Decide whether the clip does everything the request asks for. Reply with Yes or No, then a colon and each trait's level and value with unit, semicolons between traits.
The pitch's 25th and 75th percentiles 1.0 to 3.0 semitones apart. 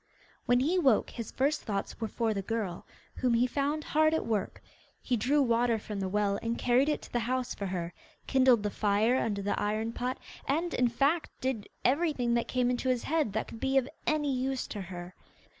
No: average, 4.1 semitones